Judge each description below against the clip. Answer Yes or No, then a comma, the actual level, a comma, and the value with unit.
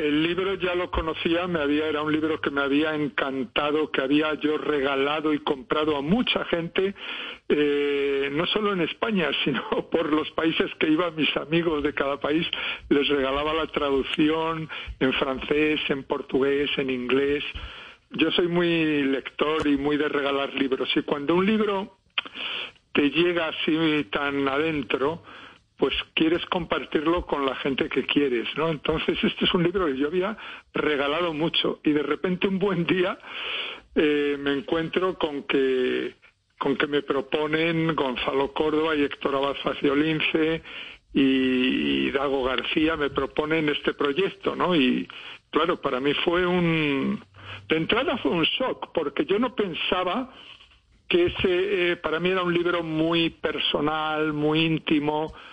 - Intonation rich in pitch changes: No, average, 3.4 semitones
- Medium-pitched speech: Yes, medium, 155 Hz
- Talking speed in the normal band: Yes, average, 155 wpm